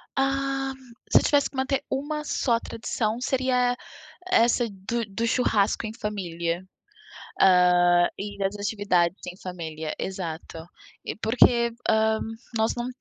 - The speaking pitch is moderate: No, high, 220 Hz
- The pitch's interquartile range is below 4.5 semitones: No, average, 5.3 semitones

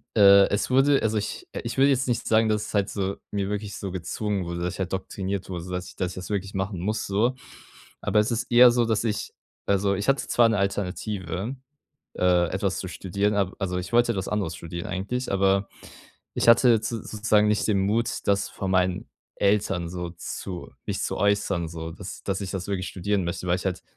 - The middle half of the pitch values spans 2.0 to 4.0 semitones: Yes, narrow, 2.6 semitones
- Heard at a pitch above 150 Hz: No, low, 100 Hz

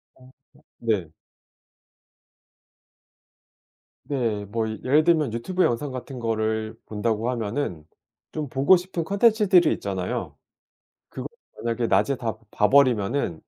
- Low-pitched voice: Yes, low, 120 Hz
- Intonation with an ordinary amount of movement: Yes, average, 5.0 semitones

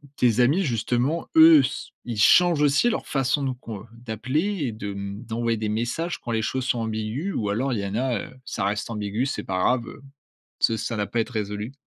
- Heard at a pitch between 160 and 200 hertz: No, low, 120 Hz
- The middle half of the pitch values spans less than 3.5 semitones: No, average, 3.8 semitones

